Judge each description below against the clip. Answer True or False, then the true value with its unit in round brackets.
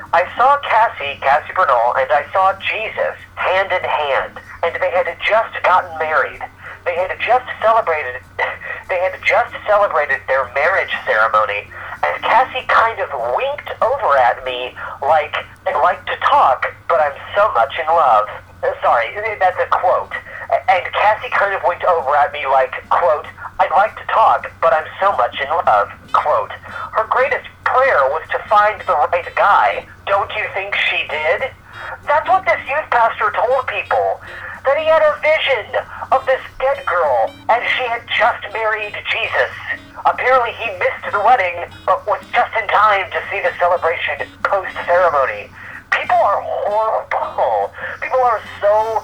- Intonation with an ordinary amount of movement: False (6.7 semitones)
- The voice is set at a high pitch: True (220 Hz)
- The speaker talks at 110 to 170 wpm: True (160 wpm)